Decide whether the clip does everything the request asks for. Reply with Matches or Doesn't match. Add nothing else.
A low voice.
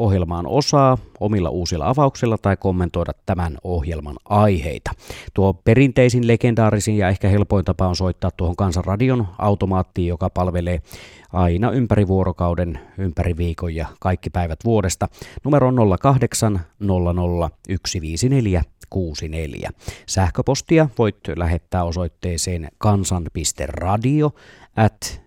Matches